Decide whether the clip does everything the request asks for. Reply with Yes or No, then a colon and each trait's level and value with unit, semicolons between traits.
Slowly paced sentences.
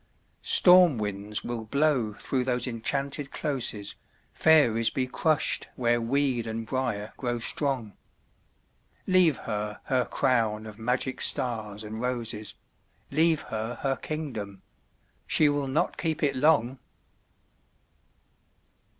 Yes: slow, 110 wpm